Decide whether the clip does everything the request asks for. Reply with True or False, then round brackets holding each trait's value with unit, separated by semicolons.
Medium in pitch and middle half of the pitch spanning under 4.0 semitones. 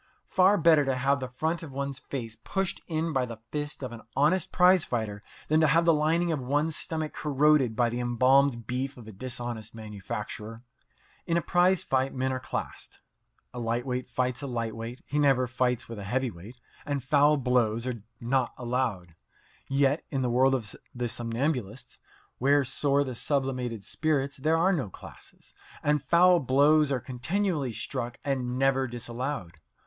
False (130 Hz; 3.6 semitones)